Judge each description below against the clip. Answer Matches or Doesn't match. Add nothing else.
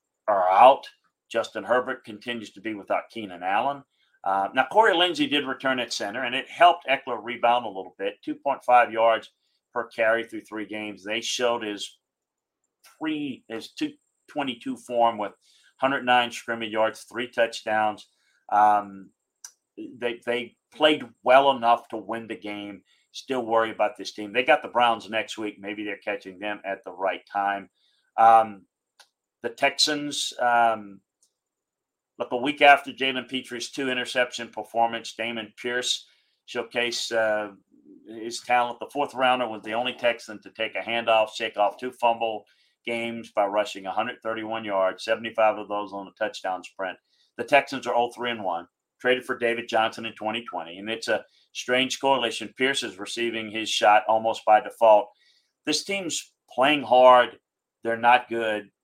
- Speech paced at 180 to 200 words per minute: Doesn't match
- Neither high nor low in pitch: Doesn't match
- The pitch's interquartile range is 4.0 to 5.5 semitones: Doesn't match